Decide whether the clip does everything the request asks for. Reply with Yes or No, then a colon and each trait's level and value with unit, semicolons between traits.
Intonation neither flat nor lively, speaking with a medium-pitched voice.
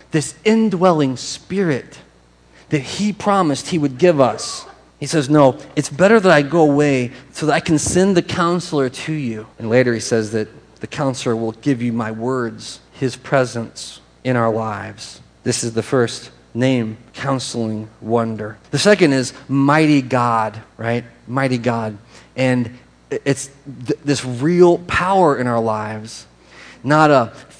No: average, 4.7 semitones; low, 130 Hz